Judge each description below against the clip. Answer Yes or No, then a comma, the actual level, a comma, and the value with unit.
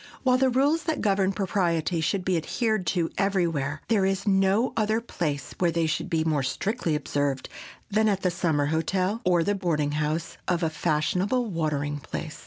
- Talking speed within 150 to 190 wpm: Yes, average, 180 wpm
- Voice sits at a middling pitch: Yes, medium, 180 Hz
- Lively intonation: No, average, 4.5 semitones